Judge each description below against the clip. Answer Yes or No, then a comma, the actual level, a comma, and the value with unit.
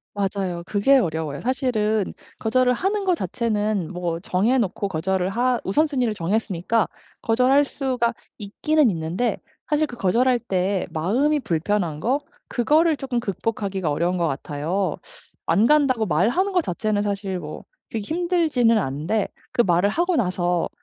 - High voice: Yes, high, 215 Hz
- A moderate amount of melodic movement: No, wide, 5.9 semitones